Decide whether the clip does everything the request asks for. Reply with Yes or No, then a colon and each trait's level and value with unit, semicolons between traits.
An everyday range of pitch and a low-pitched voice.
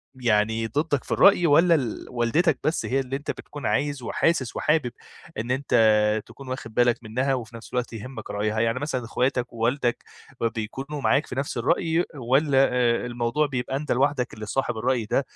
Yes: average, 3.3 semitones; low, 130 Hz